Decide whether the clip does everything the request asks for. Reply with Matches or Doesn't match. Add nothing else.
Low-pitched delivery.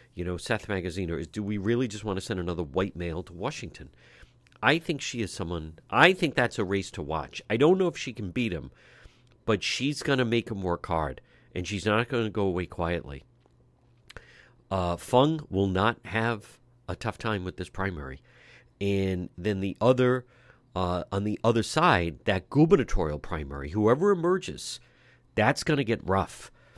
Matches